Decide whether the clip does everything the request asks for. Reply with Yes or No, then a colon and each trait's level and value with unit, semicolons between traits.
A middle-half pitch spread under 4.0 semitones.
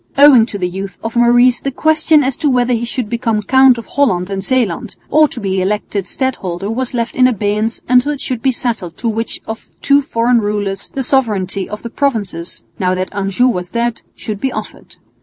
No: average, 4.3 semitones